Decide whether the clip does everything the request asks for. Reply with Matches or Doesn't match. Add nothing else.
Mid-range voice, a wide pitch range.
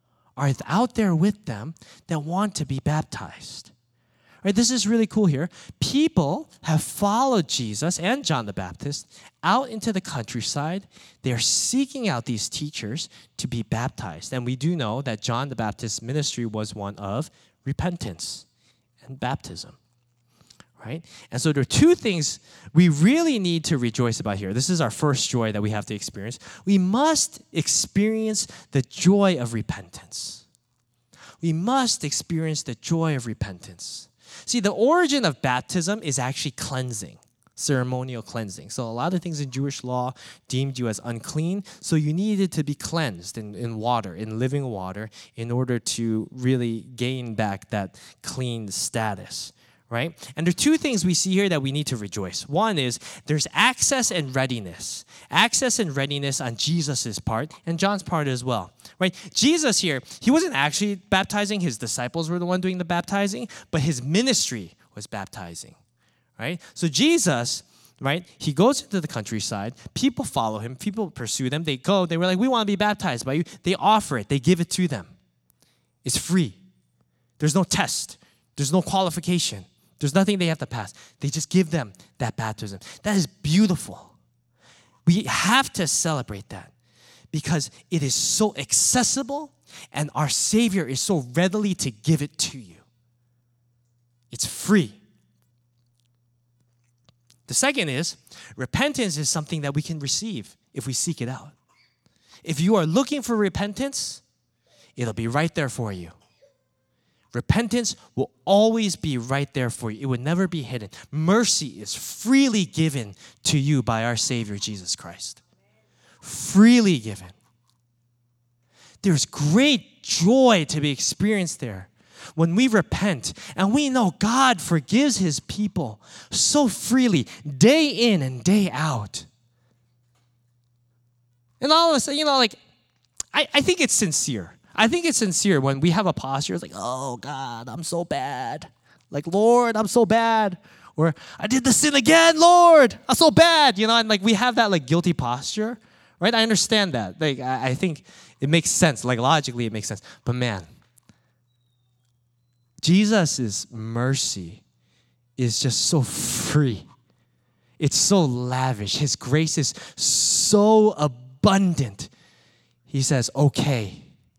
Matches